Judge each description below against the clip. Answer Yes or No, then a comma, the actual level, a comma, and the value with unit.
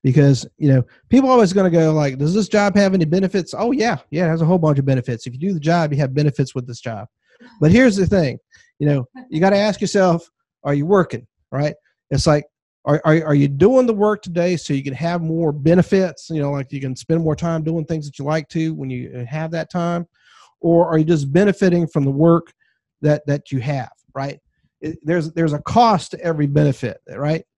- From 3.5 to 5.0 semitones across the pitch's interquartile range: Yes, average, 4.1 semitones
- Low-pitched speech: No, medium, 160 Hz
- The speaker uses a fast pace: Yes, fast, 235 wpm